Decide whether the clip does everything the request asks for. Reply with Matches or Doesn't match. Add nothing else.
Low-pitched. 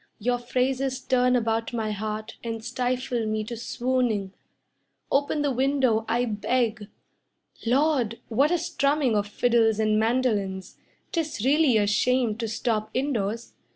Doesn't match